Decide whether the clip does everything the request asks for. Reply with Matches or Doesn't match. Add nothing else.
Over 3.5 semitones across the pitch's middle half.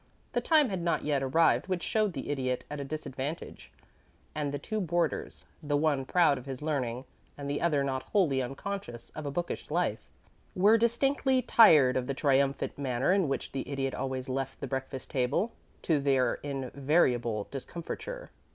Matches